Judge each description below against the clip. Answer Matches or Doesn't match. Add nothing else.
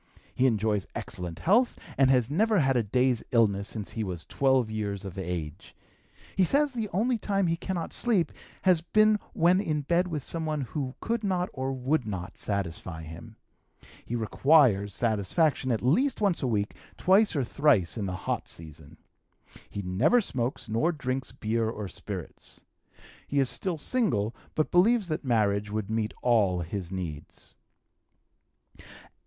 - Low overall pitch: Matches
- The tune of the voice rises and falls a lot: Matches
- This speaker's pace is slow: Doesn't match